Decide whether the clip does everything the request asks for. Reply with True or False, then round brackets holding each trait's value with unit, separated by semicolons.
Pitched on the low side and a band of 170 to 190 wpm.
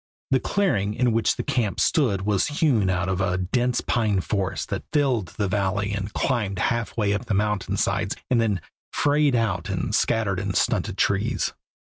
True (105 Hz; 175 wpm)